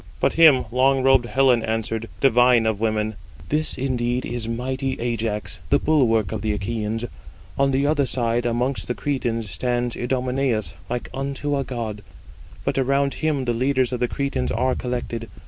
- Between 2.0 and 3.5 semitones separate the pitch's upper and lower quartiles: Yes, average, 2.7 semitones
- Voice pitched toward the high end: No, low, 125 Hz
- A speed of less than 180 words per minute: Yes, average, 165 wpm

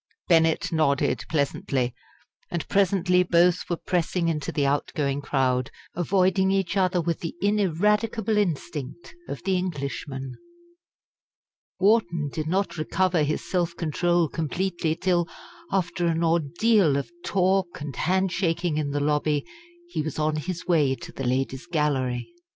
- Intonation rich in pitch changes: No, average, 3.9 semitones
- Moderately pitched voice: Yes, medium, 170 Hz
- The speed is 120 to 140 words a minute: Yes, slow, 135 wpm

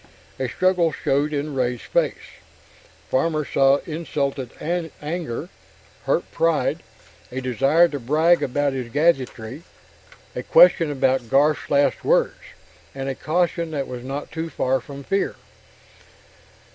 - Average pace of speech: No, slow, 125 wpm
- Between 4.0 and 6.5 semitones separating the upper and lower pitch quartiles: No, average, 3.6 semitones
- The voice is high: No, medium, 145 Hz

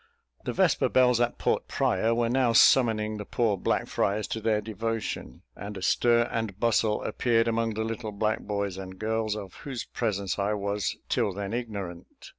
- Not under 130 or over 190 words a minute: Yes, average, 180 wpm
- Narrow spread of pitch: Yes, narrow, 2.2 semitones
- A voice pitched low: Yes, low, 110 Hz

